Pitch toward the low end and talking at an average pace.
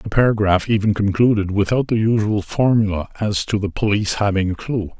Yes: low, 105 Hz; average, 180 wpm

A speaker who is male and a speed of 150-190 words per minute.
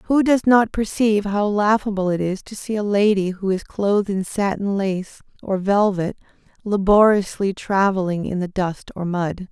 No: female; average, 170 wpm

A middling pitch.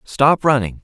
No: low, 125 Hz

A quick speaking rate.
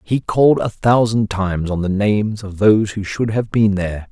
Yes: fast, 220 wpm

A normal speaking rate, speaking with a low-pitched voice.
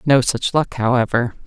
Yes: average, 165 wpm; low, 125 Hz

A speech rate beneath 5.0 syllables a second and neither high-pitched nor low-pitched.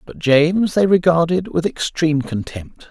Yes: 4.7 syllables/s; medium, 165 Hz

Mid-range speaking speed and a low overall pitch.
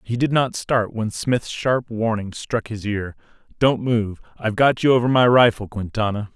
Yes: average, 190 wpm; low, 115 Hz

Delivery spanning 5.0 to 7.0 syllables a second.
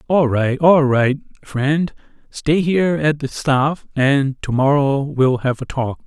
No: 3.5 syllables/s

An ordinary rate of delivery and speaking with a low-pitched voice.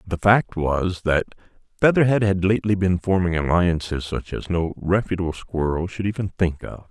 Yes: average, 165 wpm; very low, 90 Hz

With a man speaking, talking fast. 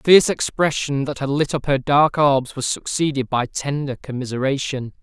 No: male; average, 180 wpm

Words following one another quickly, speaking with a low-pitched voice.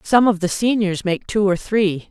No: fast, 230 wpm; high, 195 Hz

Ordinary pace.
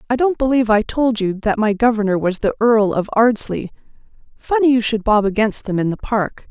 No: fast, 210 wpm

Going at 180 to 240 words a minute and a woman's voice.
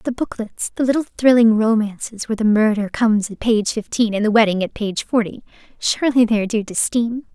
Yes: average, 195 wpm; female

